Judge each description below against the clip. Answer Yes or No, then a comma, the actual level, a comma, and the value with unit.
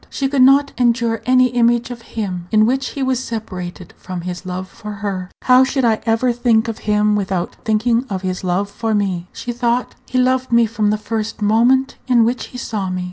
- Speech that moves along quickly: Yes, fast, 210 wpm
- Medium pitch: No, high, 225 Hz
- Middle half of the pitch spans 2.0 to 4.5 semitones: Yes, average, 3.6 semitones